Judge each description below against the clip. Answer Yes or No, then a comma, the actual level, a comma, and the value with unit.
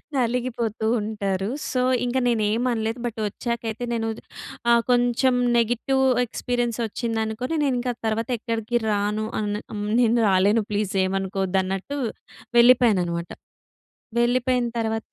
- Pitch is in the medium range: No, high, 225 Hz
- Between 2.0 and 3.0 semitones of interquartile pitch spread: Yes, average, 2.7 semitones